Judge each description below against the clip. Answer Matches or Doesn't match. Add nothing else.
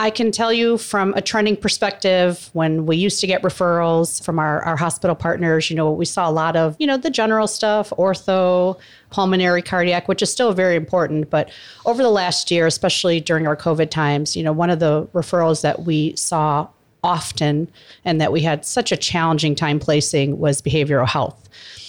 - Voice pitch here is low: Doesn't match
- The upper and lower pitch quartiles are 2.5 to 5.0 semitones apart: Matches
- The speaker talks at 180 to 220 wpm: Matches